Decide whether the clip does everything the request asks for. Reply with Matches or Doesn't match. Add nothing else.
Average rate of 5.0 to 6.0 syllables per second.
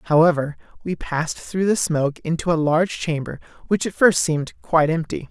Matches